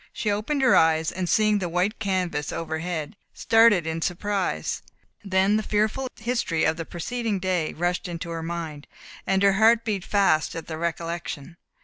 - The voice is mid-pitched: Yes, medium, 180 Hz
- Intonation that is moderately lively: Yes, average, 4.2 semitones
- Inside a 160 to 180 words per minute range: Yes, average, 165 wpm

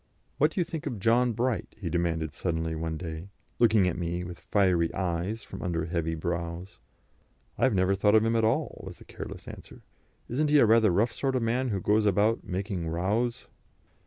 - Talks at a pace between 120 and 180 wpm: No, average, 200 wpm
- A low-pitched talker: Yes, very low, 95 Hz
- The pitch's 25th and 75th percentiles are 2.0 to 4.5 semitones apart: No, average, 5.0 semitones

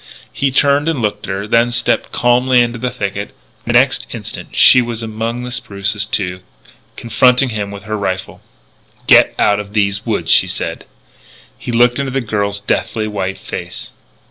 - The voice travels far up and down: No, average, 3.3 semitones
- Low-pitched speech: Yes, low, 110 Hz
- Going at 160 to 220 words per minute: Yes, average, 175 wpm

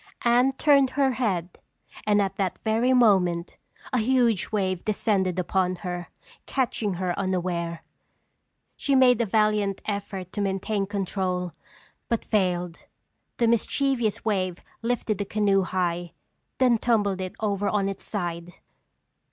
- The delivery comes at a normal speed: No, slow, 130 wpm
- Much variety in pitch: No, average, 3.8 semitones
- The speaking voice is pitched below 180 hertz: No, high, 200 Hz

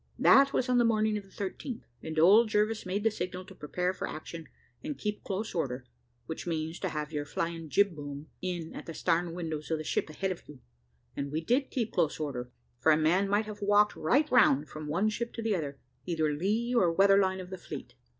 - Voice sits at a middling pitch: Yes, medium, 180 Hz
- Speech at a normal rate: No, fast, 230 wpm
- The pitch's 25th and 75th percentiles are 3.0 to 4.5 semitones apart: No, average, 5.1 semitones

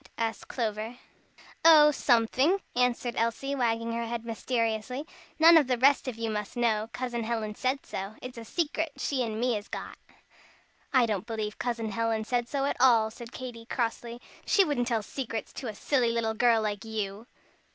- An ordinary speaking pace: Yes, average, 180 wpm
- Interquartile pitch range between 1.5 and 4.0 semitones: Yes, narrow, 2.5 semitones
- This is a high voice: Yes, high, 235 Hz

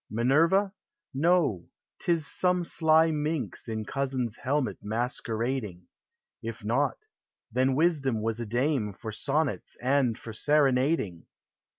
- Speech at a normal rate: No, slow, 120 wpm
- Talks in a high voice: No, low, 130 Hz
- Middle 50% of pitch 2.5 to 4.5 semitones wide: No, average, 5.2 semitones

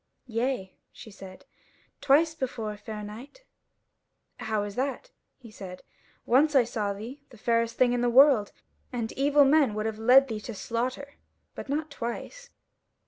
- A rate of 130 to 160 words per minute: Yes, average, 155 wpm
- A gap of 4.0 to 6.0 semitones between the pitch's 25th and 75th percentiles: Yes, average, 4.3 semitones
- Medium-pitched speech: No, high, 240 Hz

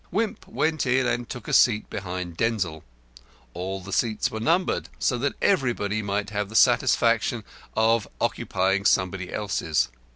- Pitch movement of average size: Yes, average, 4.3 semitones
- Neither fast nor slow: Yes, average, 150 wpm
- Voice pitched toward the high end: No, low, 105 Hz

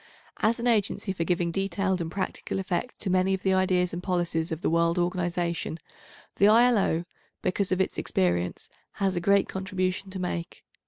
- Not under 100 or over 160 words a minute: No, average, 175 wpm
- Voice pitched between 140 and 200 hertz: Yes, medium, 185 Hz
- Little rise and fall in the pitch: Yes, narrow, 2.0 semitones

